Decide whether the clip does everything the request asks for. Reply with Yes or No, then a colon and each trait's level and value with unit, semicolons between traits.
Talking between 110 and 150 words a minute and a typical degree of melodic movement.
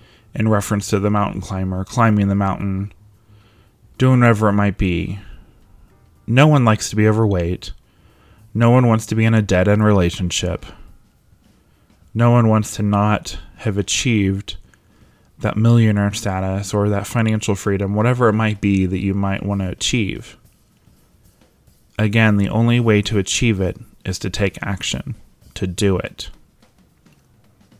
No: average, 145 wpm; narrow, 2.1 semitones